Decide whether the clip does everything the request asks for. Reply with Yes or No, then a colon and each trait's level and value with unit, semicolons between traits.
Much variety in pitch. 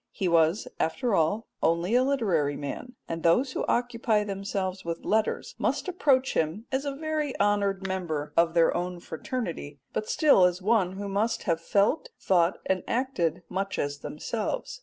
Yes: wide, 6.0 semitones